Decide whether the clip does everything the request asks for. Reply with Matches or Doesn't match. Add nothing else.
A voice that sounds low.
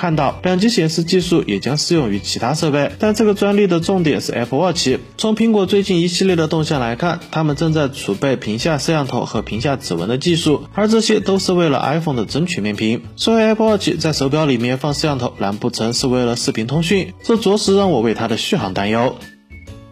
Doesn't match